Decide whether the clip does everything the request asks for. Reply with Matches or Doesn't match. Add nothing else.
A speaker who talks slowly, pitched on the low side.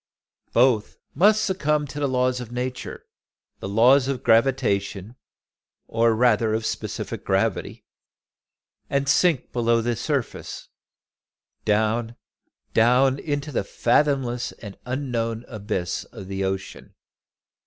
Matches